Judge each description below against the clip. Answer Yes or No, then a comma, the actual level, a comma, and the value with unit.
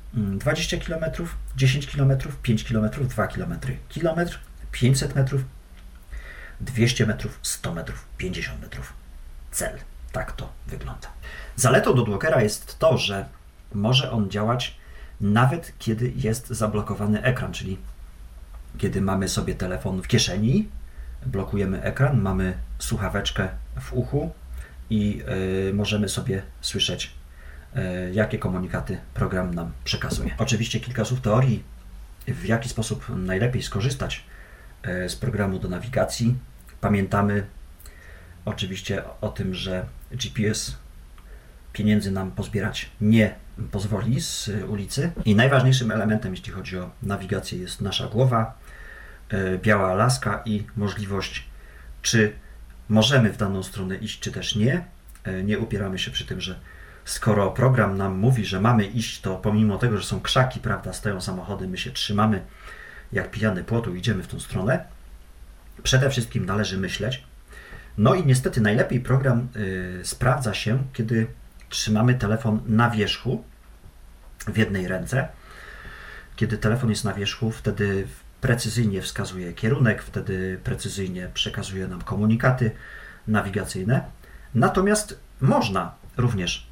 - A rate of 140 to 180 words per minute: No, average, 120 wpm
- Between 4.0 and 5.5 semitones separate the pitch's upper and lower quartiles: Yes, average, 4.3 semitones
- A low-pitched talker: Yes, low, 105 Hz